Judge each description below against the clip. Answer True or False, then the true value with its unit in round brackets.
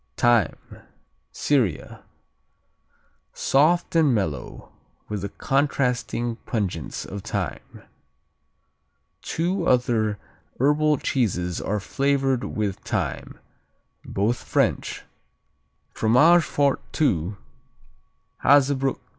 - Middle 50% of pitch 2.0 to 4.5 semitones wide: False (5.4 semitones)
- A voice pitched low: True (125 Hz)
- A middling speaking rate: False (80 wpm)